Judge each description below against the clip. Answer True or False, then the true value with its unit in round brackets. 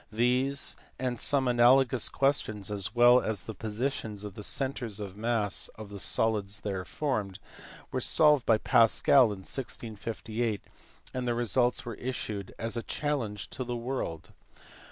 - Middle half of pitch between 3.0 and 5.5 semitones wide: True (3.5 semitones)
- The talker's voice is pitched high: False (115 Hz)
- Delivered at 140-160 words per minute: True (155 wpm)